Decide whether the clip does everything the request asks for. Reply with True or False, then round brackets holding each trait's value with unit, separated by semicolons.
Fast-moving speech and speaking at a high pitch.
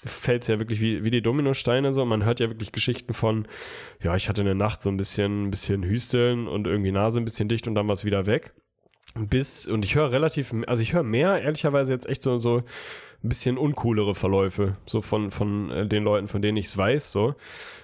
False (215 wpm; 110 Hz)